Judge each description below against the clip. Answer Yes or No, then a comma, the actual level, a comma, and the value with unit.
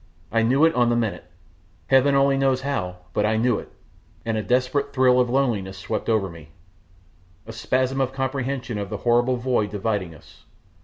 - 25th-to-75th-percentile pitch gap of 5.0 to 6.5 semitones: No, average, 3.8 semitones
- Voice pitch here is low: Yes, low, 120 Hz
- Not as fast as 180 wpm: No, average, 185 wpm